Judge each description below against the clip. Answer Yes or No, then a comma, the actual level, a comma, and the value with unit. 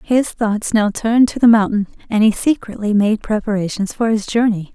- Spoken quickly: No, average, 190 wpm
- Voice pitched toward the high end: Yes, high, 215 Hz